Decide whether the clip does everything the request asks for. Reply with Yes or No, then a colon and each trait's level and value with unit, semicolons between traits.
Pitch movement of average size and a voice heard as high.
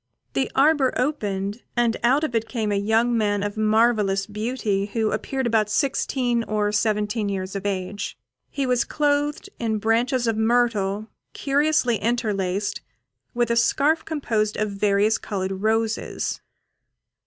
Yes: average, 3.0 semitones; high, 220 Hz